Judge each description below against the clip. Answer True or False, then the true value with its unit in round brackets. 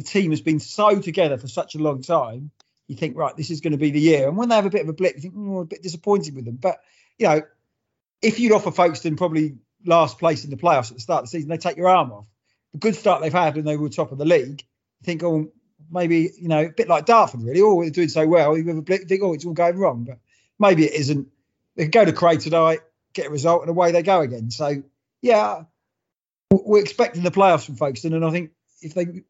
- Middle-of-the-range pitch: True (165 Hz)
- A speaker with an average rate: False (270 wpm)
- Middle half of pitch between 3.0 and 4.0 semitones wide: True (3.4 semitones)